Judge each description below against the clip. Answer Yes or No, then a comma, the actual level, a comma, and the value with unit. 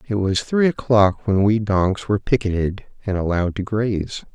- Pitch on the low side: Yes, low, 105 Hz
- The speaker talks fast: No, average, 180 wpm